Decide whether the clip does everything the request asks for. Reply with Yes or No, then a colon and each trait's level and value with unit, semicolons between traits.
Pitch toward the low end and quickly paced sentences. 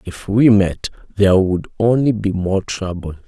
No: low, 100 Hz; average, 165 wpm